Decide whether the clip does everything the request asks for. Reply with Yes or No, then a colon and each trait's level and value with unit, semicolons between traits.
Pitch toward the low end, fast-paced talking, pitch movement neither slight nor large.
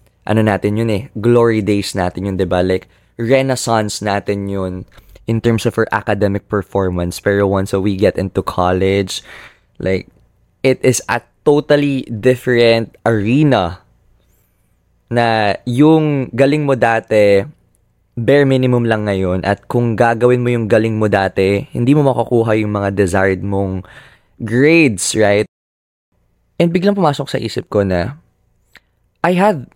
No: low, 110 Hz; average, 140 wpm; average, 4.1 semitones